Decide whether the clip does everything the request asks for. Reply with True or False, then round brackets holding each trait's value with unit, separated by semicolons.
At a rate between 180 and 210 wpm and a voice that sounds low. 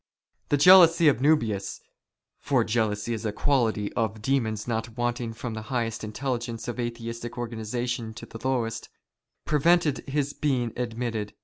False (150 wpm; 120 Hz)